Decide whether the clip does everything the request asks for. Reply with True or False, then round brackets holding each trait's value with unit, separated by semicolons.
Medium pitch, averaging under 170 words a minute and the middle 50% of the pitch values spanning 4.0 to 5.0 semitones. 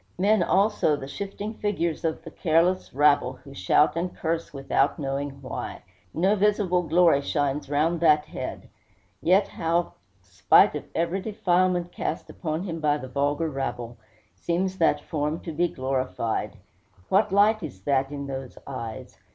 True (160 Hz; 150 wpm; 4.6 semitones)